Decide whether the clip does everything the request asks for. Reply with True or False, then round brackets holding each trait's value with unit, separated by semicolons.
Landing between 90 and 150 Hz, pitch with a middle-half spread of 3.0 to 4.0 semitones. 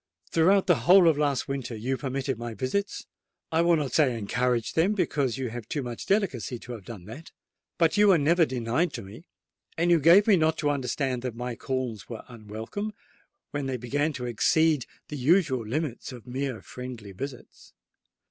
False (135 Hz; 5.1 semitones)